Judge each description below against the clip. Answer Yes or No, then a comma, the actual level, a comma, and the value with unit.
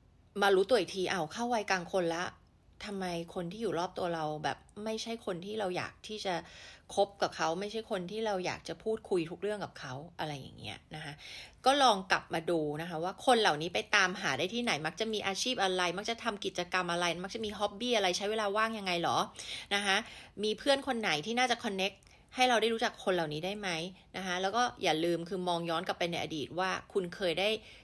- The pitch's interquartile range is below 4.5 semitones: Yes, average, 3.6 semitones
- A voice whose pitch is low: No, high, 195 Hz